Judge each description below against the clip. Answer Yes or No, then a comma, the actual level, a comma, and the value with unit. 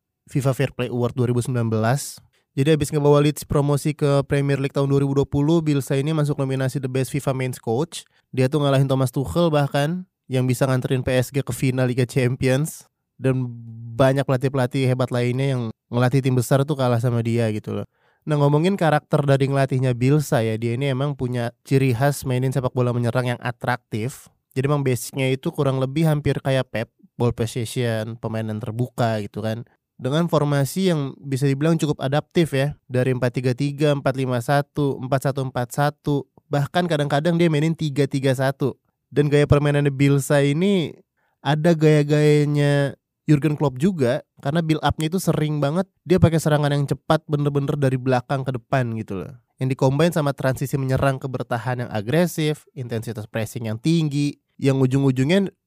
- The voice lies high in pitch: No, medium, 140 Hz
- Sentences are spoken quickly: Yes, fast, 160 wpm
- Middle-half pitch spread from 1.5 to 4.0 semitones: Yes, narrow, 2.6 semitones